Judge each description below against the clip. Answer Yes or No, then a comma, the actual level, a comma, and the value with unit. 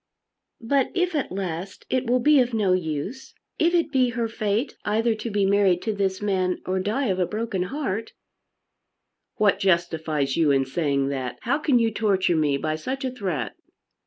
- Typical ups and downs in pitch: No, wide, 5.8 semitones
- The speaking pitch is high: Yes, high, 200 Hz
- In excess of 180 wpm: Yes, average, 190 wpm